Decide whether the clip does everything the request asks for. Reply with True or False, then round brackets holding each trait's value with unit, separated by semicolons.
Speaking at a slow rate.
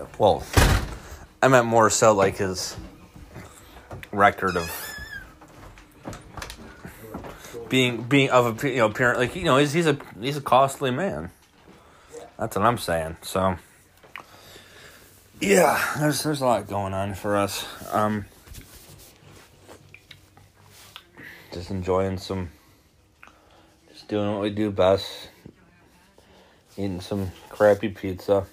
True (115 wpm)